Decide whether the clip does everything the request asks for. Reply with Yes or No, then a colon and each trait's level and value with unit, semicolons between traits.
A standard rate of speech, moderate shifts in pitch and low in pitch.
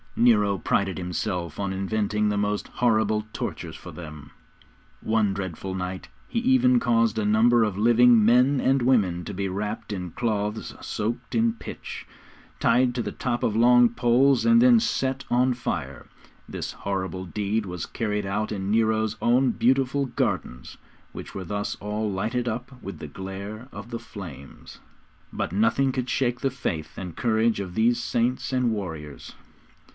Yes: average, 160 wpm; average, 3.9 semitones; low, 110 Hz